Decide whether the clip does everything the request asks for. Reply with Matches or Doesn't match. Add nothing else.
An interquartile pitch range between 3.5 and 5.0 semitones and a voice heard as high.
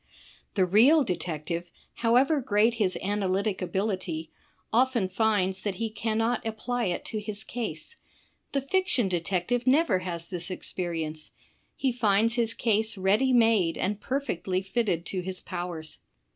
Matches